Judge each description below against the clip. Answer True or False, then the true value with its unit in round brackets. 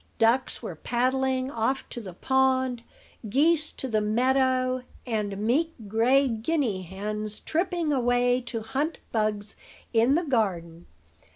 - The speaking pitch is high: True (245 Hz)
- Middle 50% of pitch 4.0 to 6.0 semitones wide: False (3.6 semitones)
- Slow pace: True (125 wpm)